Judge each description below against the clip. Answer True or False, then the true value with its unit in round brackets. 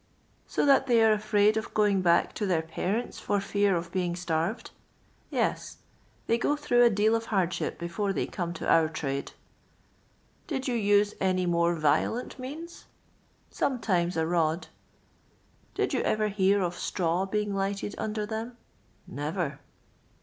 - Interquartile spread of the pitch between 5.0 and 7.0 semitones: False (4.1 semitones)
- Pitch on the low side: False (200 Hz)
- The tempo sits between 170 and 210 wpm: True (180 wpm)